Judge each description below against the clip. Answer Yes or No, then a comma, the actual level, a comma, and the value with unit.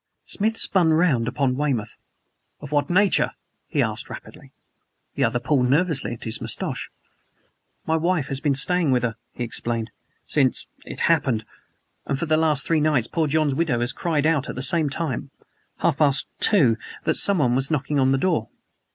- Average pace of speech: Yes, average, 175 wpm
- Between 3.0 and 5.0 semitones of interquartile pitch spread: Yes, average, 4.1 semitones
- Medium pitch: Yes, medium, 145 Hz